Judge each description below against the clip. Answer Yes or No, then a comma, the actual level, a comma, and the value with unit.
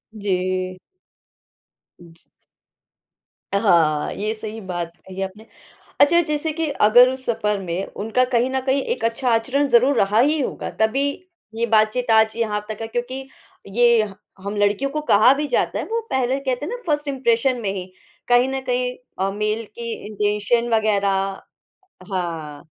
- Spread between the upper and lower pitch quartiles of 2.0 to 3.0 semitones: No, average, 4.4 semitones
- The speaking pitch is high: Yes, high, 225 Hz